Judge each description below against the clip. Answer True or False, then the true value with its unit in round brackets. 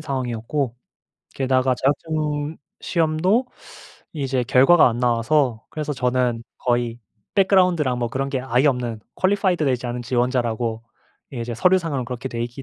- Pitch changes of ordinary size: True (4.1 semitones)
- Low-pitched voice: True (130 Hz)